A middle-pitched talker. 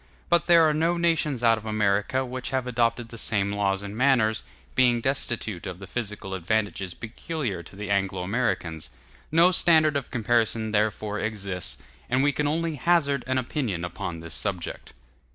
No: low, 115 Hz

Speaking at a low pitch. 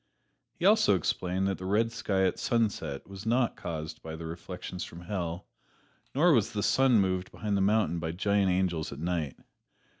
Yes: very low, 95 Hz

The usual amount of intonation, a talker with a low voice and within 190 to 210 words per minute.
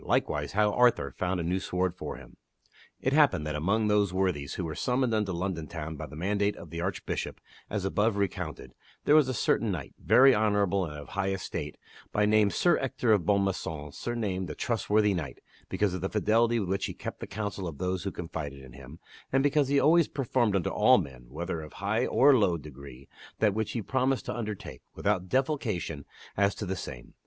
Yes: average, 4.7 semitones; low, 100 Hz; fast, 205 wpm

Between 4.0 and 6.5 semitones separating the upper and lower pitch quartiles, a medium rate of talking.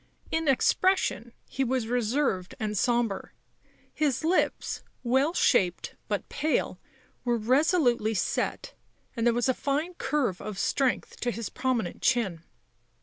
No: average, 4.3 semitones; slow, 130 wpm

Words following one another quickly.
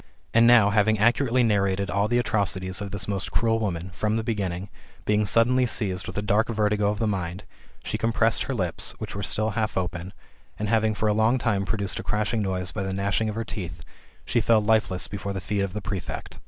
Yes: fast, 220 wpm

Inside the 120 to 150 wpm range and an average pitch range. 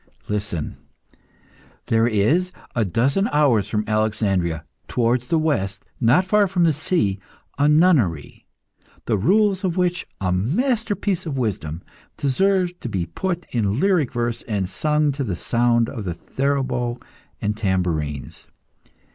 No: slow, 135 wpm; wide, 8.9 semitones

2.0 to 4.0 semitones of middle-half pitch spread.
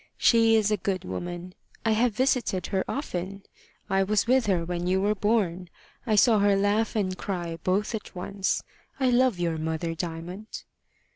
Yes: average, 3.6 semitones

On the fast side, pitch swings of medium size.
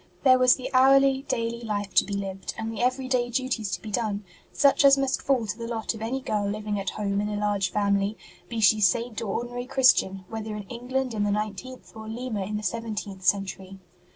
Yes: fast, 215 wpm; average, 3.5 semitones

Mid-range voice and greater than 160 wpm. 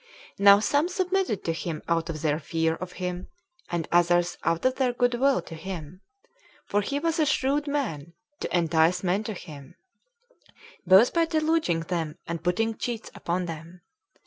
Yes: medium, 180 Hz; average, 170 wpm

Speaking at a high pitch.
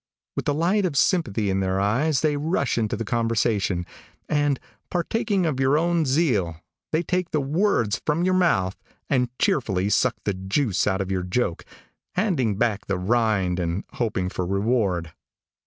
No: low, 115 Hz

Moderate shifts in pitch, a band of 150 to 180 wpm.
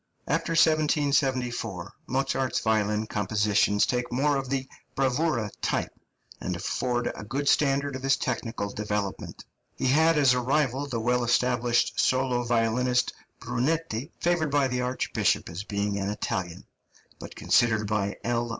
No: average, 4.0 semitones; average, 140 wpm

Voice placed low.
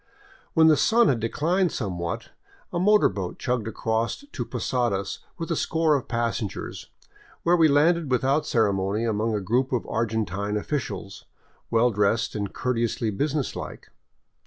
Yes: low, 120 Hz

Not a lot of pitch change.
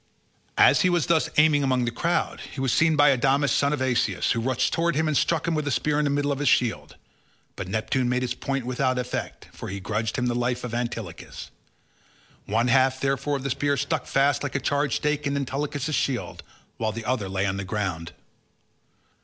No: average, 3.3 semitones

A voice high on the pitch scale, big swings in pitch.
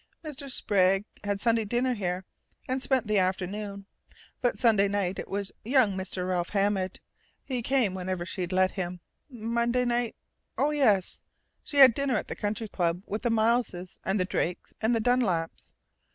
No: high, 205 Hz; average, 4.4 semitones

